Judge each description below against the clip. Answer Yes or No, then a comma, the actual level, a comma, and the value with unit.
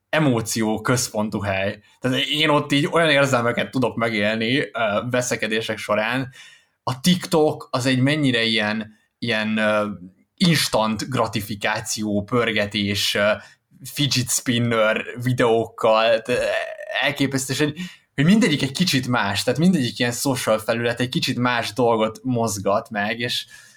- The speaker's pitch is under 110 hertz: No, low, 120 Hz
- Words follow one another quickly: No, average, 110 wpm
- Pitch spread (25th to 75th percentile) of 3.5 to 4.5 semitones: Yes, average, 4.2 semitones